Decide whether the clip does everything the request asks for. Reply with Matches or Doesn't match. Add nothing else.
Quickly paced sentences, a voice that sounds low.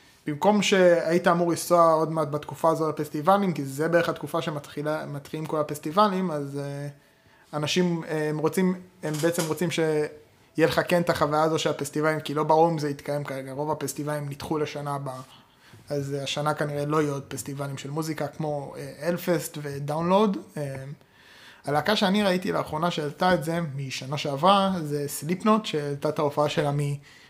Doesn't match